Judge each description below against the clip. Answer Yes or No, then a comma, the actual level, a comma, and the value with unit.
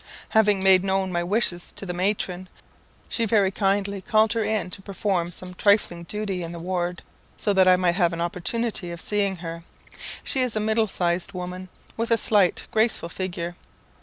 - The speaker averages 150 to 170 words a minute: No, average, 185 wpm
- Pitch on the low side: No, high, 190 Hz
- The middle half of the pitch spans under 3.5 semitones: Yes, average, 2.9 semitones